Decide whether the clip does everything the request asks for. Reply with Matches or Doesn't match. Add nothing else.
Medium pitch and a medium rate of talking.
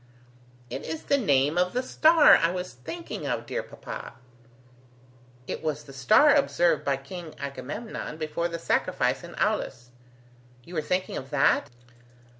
Matches